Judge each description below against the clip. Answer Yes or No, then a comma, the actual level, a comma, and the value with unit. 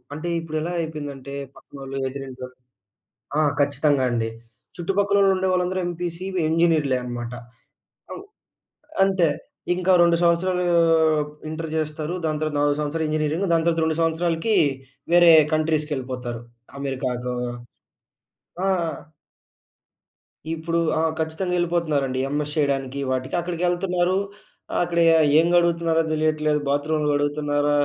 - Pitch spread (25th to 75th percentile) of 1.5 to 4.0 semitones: Yes, average, 3.2 semitones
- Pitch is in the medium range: Yes, medium, 155 Hz